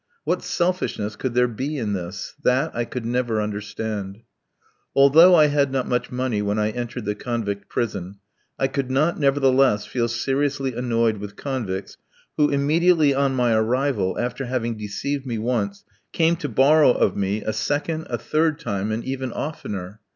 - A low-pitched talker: Yes, low, 125 Hz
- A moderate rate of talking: Yes, average, 165 wpm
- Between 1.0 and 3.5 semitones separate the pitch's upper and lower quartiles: No, average, 4.6 semitones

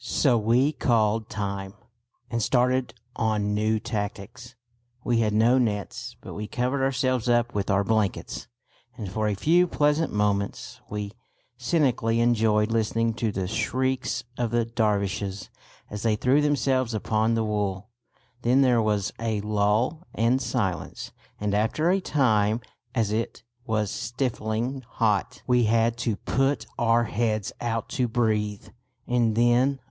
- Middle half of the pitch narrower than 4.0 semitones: Yes, average, 2.7 semitones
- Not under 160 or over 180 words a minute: No, average, 140 wpm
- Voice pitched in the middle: No, low, 115 Hz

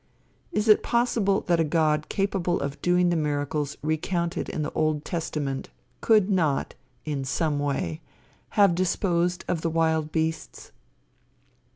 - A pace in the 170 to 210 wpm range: No, average, 140 wpm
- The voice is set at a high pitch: No, medium, 165 Hz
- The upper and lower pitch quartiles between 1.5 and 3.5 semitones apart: Yes, average, 2.9 semitones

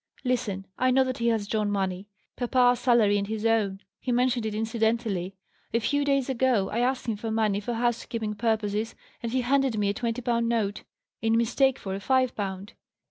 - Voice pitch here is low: No, high, 225 Hz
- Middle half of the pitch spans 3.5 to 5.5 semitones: No, average, 3.1 semitones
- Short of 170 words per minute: No, average, 195 wpm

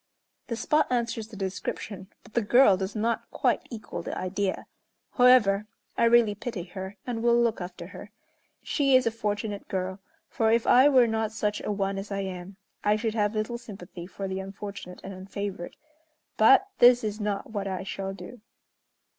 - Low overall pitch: No, high, 210 Hz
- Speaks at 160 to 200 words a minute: Yes, average, 180 wpm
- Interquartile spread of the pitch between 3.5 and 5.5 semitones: No, average, 3.0 semitones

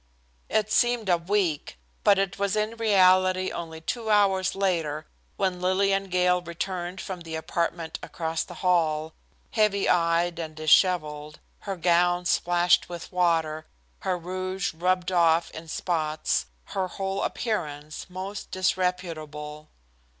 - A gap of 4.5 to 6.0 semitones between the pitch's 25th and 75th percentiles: No, average, 2.7 semitones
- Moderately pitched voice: Yes, medium, 180 Hz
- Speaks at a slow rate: Yes, slow, 130 wpm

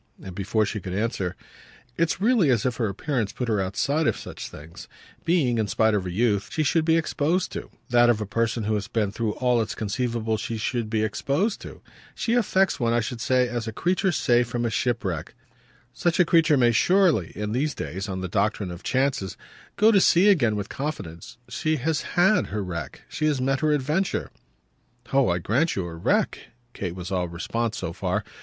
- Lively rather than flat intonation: Yes, wide, 6.7 semitones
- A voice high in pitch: No, low, 120 Hz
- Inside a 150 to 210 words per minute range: Yes, average, 195 wpm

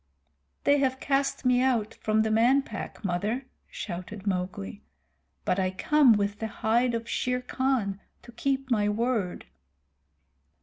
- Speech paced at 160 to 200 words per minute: No, average, 140 wpm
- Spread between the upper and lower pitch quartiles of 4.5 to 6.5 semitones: No, average, 4.1 semitones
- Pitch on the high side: Yes, high, 225 Hz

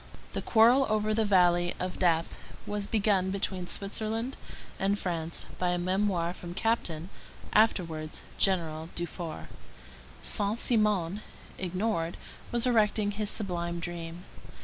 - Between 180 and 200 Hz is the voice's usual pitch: Yes, high, 190 Hz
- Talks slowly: Yes, slow, 120 wpm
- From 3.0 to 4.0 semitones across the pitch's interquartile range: Yes, average, 3.6 semitones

